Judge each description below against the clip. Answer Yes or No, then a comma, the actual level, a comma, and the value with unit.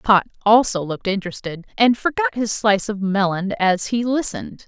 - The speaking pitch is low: No, high, 210 Hz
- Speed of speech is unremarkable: Yes, average, 165 wpm